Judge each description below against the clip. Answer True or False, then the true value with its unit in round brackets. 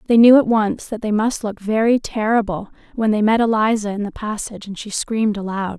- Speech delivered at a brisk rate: True (220 wpm)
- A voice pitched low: False (215 Hz)